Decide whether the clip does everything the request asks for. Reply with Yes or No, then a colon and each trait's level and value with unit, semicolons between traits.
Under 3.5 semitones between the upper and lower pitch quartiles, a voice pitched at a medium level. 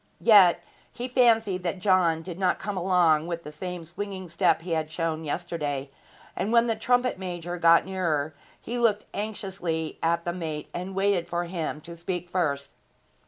Yes: average, 2.9 semitones; medium, 175 Hz